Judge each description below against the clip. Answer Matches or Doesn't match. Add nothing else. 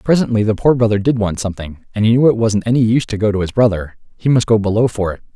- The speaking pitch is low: Matches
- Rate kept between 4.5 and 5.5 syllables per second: Doesn't match